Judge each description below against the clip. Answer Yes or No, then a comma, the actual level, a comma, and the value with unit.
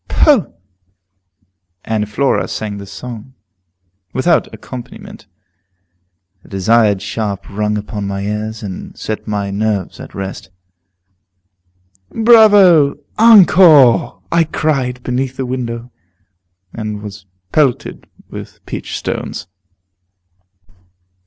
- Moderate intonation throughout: No, wide, 5.9 semitones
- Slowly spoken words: Yes, slow, 95 wpm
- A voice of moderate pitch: No, low, 115 Hz